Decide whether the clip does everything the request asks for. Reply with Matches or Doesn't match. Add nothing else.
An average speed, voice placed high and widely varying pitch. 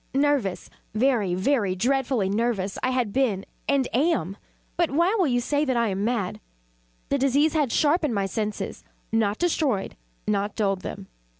Matches